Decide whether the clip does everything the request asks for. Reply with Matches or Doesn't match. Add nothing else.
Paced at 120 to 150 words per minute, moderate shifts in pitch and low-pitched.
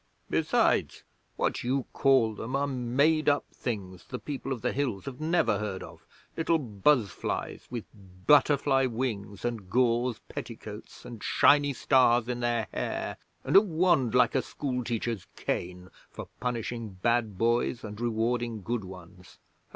Matches